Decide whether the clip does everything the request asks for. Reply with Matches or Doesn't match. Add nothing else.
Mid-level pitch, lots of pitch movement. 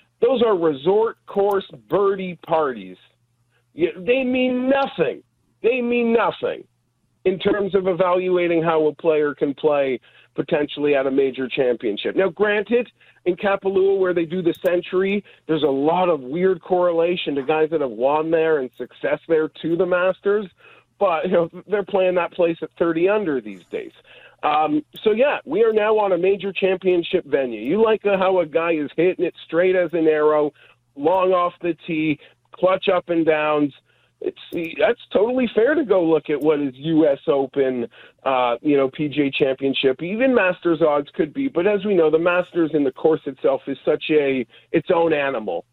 Doesn't match